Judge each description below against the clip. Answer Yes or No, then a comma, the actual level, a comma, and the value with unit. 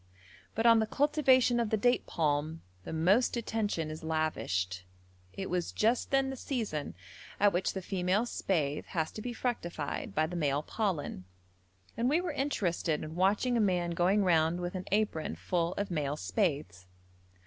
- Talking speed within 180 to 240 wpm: No, average, 170 wpm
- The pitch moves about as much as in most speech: No, wide, 6.2 semitones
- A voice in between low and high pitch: Yes, medium, 180 Hz